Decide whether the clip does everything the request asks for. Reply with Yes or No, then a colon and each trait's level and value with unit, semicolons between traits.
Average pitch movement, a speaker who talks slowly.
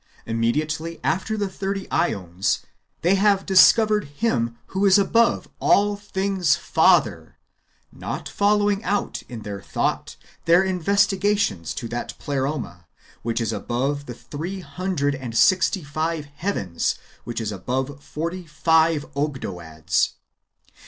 No: wide, 8.2 semitones; slow, 120 wpm